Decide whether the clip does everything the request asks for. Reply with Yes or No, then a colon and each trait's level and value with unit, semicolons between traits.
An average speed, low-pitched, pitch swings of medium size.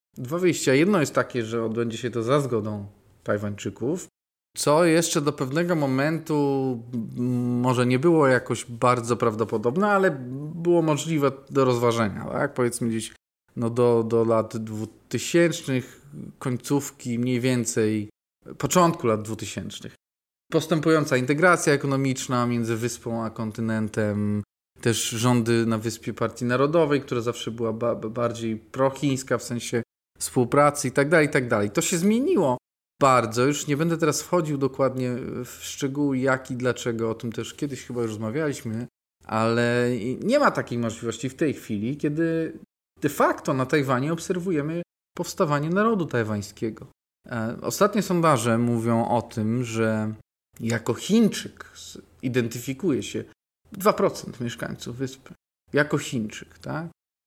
Yes: average, 130 wpm; low, 125 Hz; average, 4.4 semitones